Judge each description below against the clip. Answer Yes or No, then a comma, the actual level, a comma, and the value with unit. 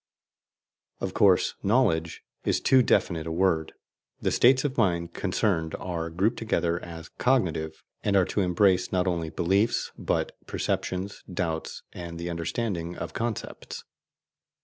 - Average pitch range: Yes, average, 3.6 semitones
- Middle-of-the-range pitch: No, very low, 90 Hz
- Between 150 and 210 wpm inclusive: No, slow, 135 wpm